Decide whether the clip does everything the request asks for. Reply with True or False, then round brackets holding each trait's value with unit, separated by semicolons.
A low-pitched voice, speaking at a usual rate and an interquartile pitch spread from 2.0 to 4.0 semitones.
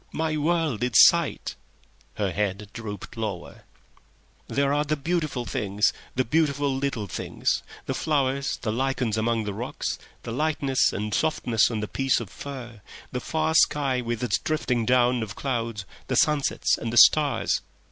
False (125 Hz; 155 wpm; 4.5 semitones)